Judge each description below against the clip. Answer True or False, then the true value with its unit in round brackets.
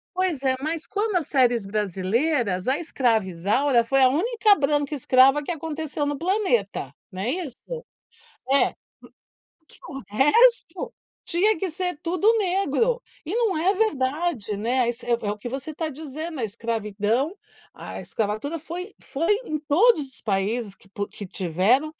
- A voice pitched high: True (280 Hz)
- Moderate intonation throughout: False (7.0 semitones)